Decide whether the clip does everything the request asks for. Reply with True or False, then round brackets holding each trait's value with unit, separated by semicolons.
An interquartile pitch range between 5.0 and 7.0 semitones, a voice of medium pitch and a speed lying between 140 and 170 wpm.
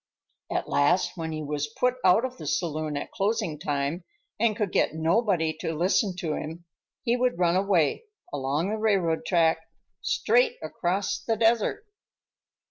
True (5.6 semitones; 180 Hz; 150 wpm)